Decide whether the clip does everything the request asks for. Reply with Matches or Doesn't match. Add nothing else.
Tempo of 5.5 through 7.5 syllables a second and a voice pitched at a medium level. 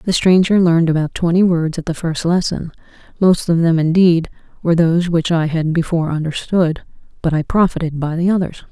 Matches